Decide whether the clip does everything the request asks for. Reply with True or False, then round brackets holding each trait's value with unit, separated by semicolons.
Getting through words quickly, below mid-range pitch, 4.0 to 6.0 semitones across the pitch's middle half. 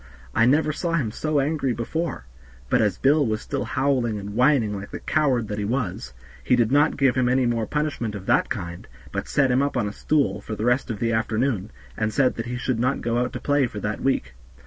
True (235 wpm; 125 Hz; 4.4 semitones)